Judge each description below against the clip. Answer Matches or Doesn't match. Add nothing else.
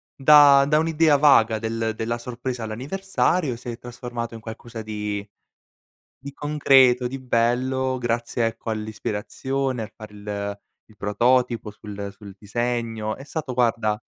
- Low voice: Matches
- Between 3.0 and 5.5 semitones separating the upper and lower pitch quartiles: Matches